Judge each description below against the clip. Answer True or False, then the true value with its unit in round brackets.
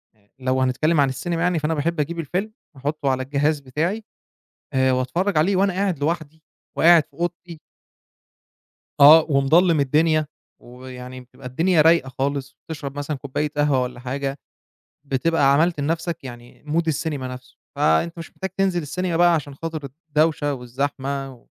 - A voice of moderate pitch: True (150 Hz)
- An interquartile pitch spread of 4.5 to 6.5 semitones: False (3.9 semitones)